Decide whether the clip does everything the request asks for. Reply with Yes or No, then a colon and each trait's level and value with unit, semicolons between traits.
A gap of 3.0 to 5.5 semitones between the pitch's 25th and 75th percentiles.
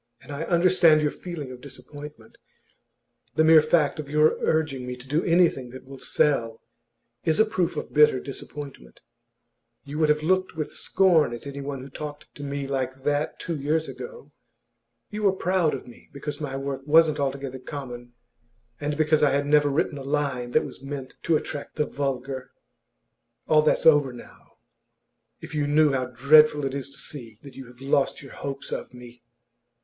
No: narrow, 2.4 semitones